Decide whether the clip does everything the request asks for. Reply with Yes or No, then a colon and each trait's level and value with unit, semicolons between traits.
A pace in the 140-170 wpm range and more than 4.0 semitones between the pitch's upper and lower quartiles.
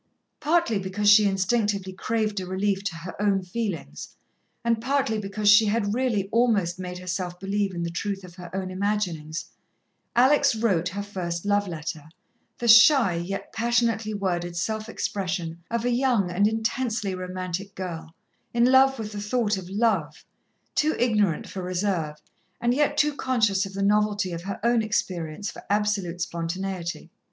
No: average, 160 wpm; average, 3.5 semitones